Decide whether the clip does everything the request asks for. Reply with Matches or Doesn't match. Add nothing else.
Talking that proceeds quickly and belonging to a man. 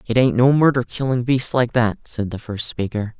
Matches